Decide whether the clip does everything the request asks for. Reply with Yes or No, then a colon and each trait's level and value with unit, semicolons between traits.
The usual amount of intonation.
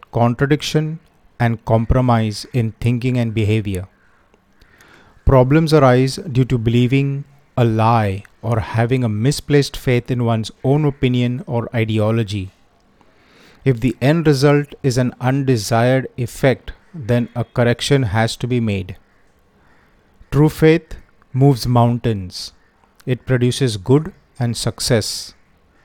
Yes: average, 3.5 semitones